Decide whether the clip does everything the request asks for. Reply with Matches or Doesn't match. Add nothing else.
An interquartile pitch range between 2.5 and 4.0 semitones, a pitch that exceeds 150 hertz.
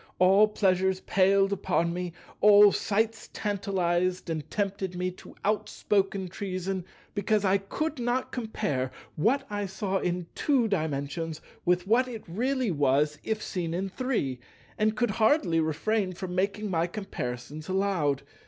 Matches